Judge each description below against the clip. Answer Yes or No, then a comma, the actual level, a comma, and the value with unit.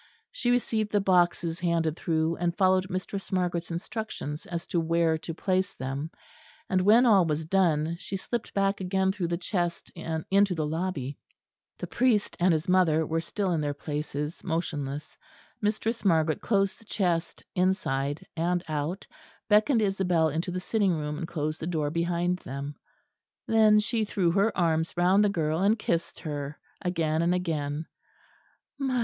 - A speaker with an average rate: Yes, average, 160 wpm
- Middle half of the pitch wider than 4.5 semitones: No, average, 3.3 semitones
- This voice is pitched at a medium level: Yes, medium, 175 Hz